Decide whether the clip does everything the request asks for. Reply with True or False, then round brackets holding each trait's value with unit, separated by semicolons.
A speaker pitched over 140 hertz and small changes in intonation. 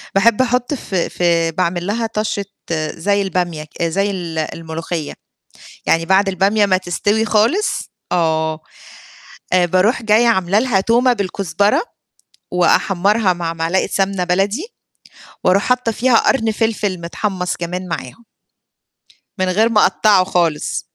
False (190 Hz; 3.7 semitones)